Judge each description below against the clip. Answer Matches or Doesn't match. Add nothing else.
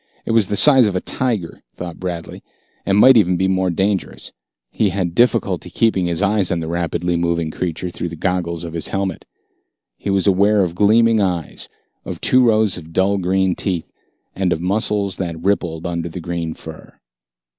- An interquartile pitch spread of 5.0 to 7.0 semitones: Doesn't match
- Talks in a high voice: Doesn't match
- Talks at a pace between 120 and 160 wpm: Doesn't match